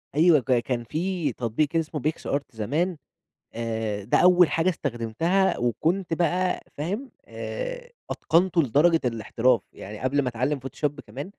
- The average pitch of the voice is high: No, medium, 150 Hz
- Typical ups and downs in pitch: No, wide, 6.6 semitones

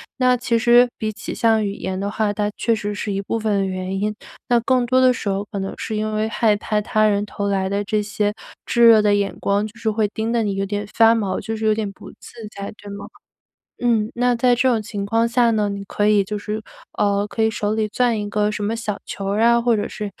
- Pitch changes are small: Yes, narrow, 2.0 semitones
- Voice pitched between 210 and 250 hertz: Yes, high, 215 Hz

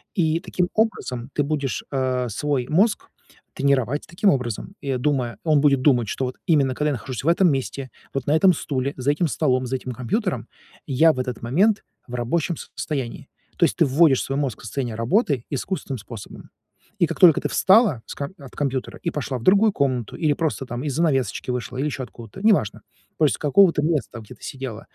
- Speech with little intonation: No, average, 4.1 semitones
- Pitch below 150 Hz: Yes, medium, 140 Hz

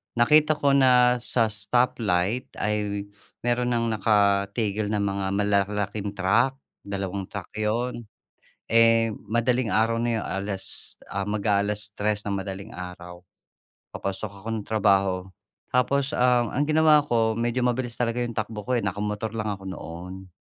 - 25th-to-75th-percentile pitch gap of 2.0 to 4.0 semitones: Yes, average, 3.2 semitones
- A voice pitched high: No, low, 105 Hz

